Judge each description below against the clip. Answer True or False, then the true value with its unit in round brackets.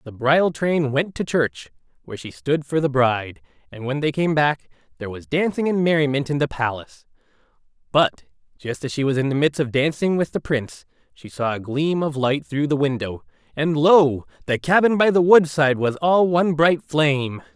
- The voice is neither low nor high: True (145 Hz)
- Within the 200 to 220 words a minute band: True (205 wpm)